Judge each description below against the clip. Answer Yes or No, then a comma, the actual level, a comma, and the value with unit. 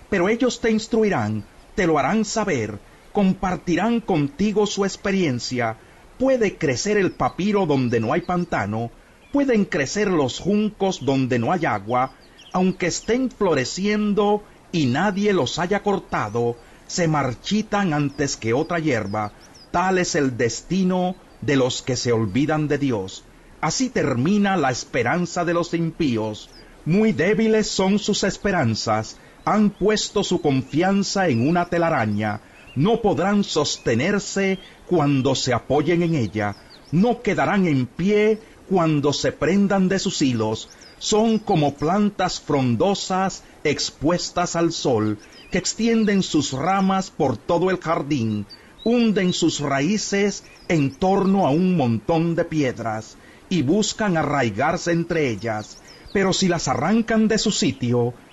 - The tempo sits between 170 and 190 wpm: No, average, 130 wpm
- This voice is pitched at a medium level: Yes, medium, 175 Hz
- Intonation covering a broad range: Yes, wide, 7.2 semitones